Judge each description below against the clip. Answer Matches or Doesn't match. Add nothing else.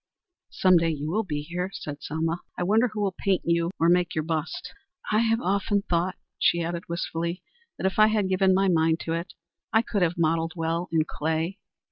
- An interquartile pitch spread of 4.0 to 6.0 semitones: Doesn't match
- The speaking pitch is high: Doesn't match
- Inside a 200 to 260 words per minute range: Matches